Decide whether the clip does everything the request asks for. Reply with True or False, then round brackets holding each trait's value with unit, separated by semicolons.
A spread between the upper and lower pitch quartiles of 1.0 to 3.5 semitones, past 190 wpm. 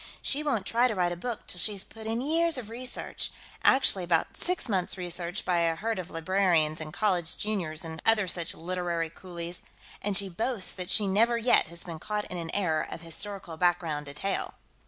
False (4.3 semitones; 200 wpm)